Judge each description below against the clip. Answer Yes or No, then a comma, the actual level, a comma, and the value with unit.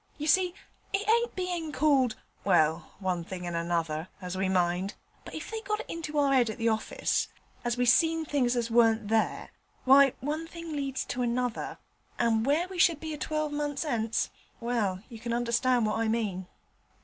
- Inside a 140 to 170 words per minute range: No, average, 185 wpm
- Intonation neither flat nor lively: No, wide, 5.8 semitones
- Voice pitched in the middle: No, high, 245 Hz